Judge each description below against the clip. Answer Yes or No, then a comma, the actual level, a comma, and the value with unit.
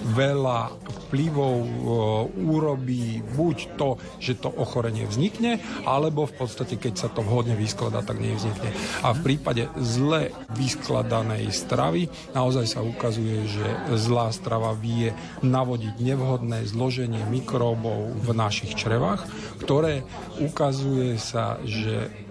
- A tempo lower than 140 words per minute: Yes, average, 115 wpm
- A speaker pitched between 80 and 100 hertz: No, low, 120 Hz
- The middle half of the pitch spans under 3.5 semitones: Yes, average, 2.9 semitones